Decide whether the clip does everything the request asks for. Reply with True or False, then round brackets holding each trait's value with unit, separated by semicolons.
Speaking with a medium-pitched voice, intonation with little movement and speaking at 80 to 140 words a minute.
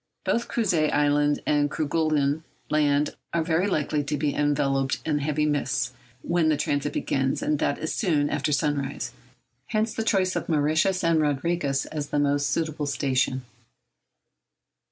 True (150 Hz; 2.0 semitones; 135 wpm)